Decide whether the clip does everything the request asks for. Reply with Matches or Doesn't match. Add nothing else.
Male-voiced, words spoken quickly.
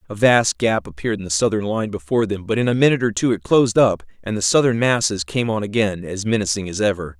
Matches